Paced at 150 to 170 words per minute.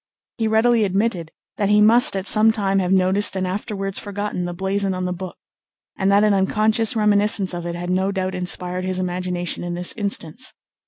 No: average, 195 wpm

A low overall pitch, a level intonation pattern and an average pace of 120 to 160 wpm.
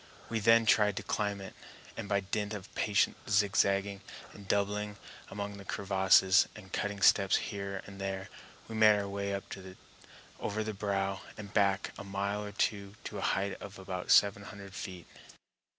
No: low, 100 Hz; narrow, 0.9 semitones; average, 170 wpm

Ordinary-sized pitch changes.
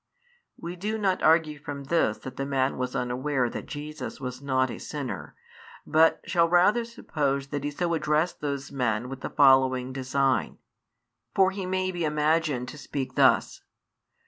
Yes: average, 4.0 semitones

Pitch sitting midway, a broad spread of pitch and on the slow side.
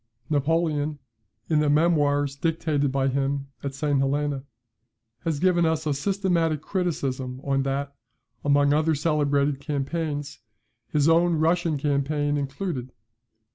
No: medium, 145 Hz; narrow, 2.5 semitones; slow, 120 wpm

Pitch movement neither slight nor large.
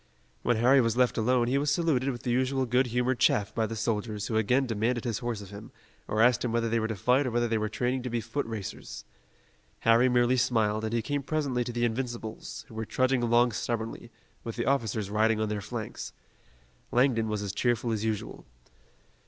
No: narrow, 2.2 semitones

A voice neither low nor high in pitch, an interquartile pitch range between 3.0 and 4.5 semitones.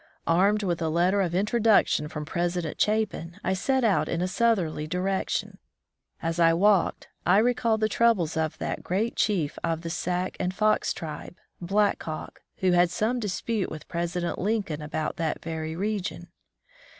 Yes: medium, 180 Hz; average, 4.0 semitones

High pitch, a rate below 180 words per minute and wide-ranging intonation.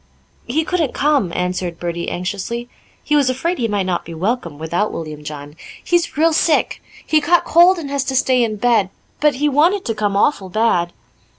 No: high, 235 Hz; average, 190 wpm; wide, 8.7 semitones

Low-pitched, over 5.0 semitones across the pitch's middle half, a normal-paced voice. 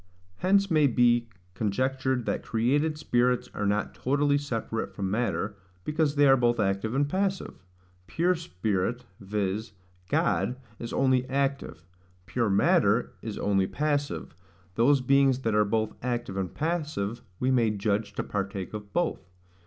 Yes: low, 120 Hz; wide, 5.4 semitones; average, 145 wpm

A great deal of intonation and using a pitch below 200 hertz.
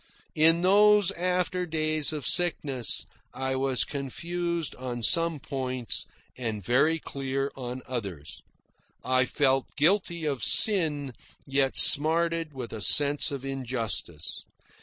No: average, 4.5 semitones; medium, 140 Hz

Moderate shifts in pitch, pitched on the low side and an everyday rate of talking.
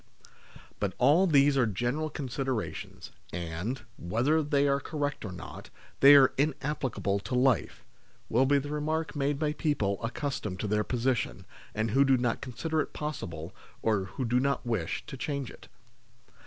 Yes: average, 4.4 semitones; low, 130 Hz; average, 170 wpm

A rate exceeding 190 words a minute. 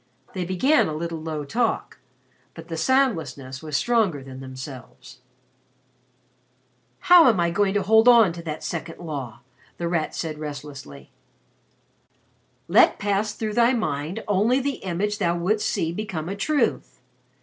No: average, 145 wpm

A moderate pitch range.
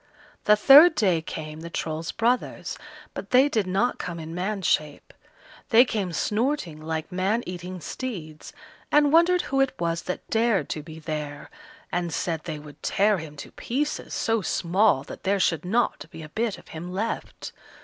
No: wide, 6.0 semitones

